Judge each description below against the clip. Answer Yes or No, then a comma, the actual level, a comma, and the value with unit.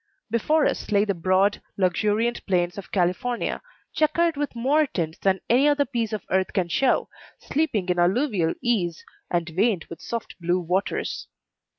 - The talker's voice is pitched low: No, high, 200 Hz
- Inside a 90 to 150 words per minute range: No, average, 160 wpm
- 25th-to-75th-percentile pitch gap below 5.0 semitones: No, wide, 5.4 semitones